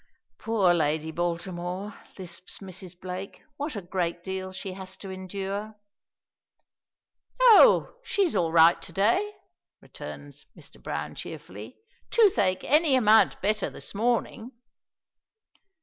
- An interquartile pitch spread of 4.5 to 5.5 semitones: No, average, 4.0 semitones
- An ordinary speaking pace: No, slow, 115 wpm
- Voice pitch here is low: No, high, 190 Hz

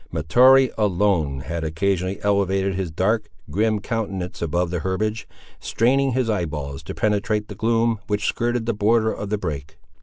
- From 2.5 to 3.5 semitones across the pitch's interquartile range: No, average, 4.2 semitones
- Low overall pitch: Yes, low, 100 Hz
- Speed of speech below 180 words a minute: Yes, average, 160 wpm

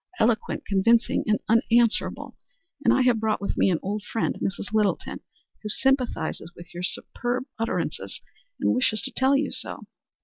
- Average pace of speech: Yes, average, 160 wpm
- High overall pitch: Yes, high, 225 Hz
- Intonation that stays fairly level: No, average, 3.3 semitones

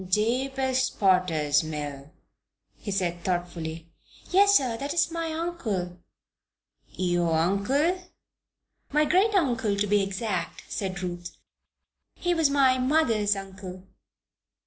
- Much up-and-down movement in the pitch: Yes, wide, 7.9 semitones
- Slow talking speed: Yes, slow, 110 wpm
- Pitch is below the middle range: No, high, 205 Hz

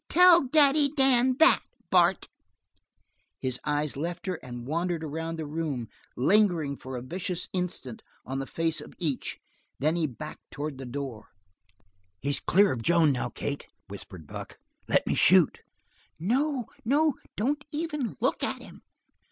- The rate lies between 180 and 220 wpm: No, average, 150 wpm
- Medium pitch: Yes, medium, 165 Hz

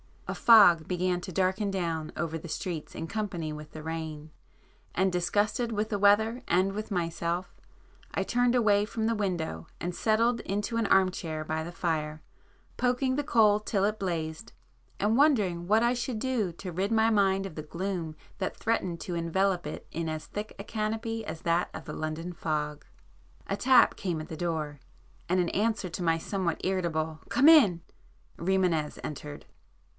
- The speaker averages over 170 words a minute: Yes, average, 180 wpm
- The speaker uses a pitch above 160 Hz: Yes, medium, 185 Hz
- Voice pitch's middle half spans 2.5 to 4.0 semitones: No, average, 4.7 semitones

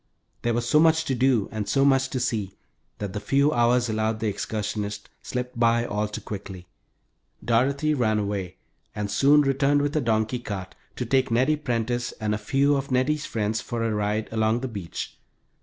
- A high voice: No, low, 115 Hz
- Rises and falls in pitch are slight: No, average, 4.0 semitones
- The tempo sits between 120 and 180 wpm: No, average, 190 wpm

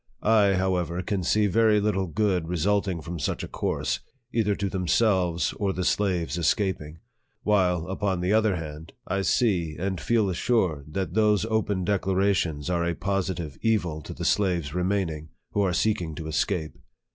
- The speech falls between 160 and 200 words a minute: Yes, average, 170 wpm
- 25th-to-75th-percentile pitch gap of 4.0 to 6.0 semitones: No, average, 3.3 semitones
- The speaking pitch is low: Yes, very low, 95 Hz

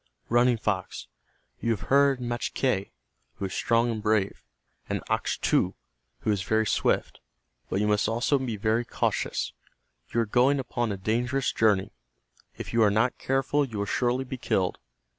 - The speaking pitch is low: Yes, low, 115 Hz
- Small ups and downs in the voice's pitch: No, average, 3.0 semitones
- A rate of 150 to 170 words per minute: Yes, average, 160 wpm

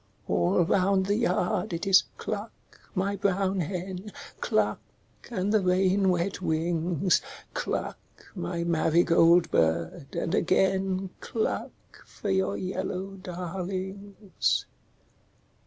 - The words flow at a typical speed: No, slow, 105 wpm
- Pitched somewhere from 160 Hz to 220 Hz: Yes, medium, 185 Hz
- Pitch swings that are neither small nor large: No, narrow, 2.2 semitones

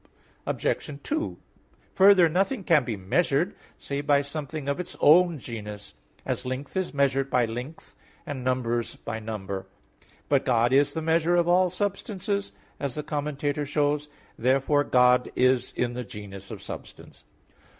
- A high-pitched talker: No, medium, 140 Hz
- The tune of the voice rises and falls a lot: No, average, 4.5 semitones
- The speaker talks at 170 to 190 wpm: No, average, 155 wpm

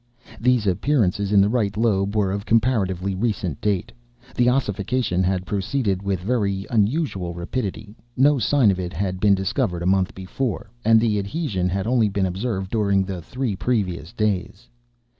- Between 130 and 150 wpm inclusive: No, average, 160 wpm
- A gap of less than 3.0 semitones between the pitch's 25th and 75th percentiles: No, average, 3.5 semitones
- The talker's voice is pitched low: Yes, low, 100 Hz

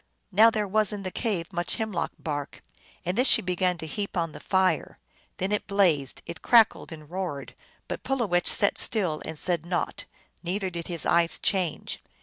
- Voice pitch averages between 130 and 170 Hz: No, medium, 180 Hz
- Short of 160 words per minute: No, average, 180 wpm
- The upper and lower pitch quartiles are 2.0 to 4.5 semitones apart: Yes, average, 3.3 semitones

